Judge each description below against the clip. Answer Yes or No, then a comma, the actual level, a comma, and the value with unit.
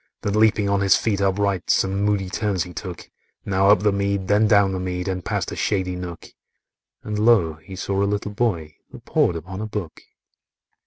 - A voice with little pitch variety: Yes, narrow, 2.0 semitones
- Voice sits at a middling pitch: No, low, 100 Hz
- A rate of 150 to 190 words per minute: No, average, 200 wpm